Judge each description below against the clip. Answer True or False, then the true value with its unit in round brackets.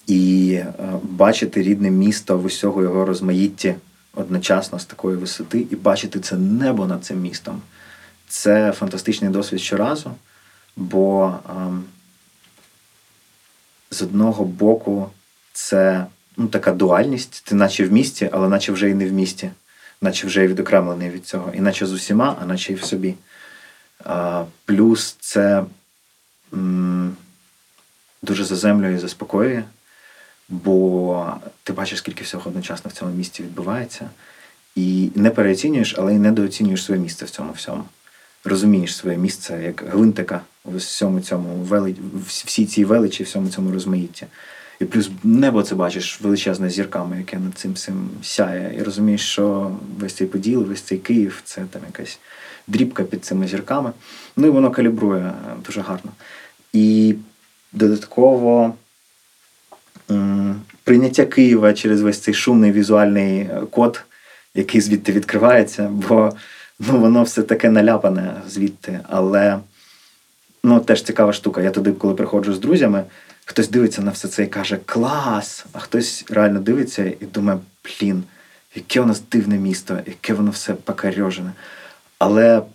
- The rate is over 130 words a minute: True (140 wpm)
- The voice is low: True (100 Hz)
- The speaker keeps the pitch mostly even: True (2.3 semitones)